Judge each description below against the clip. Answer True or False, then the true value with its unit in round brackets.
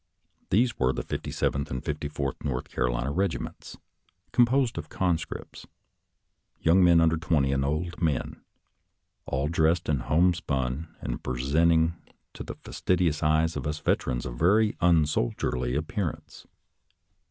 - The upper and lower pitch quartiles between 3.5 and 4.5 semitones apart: True (4.0 semitones)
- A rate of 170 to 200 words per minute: False (140 wpm)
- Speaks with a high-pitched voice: False (80 Hz)